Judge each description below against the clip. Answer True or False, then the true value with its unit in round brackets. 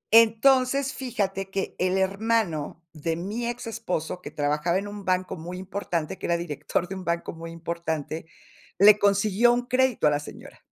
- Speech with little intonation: False (4.9 semitones)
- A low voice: False (190 Hz)